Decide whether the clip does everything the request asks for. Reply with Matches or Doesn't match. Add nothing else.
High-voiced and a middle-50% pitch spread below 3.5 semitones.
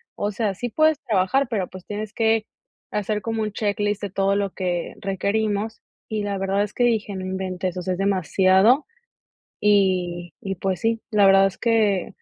Matches